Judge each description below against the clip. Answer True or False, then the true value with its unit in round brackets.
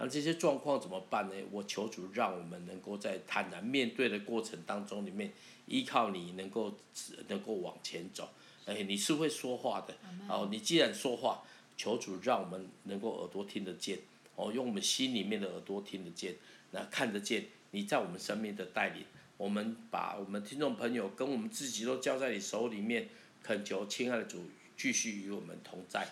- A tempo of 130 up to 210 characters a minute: False (285 characters per minute)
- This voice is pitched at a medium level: False (120 Hz)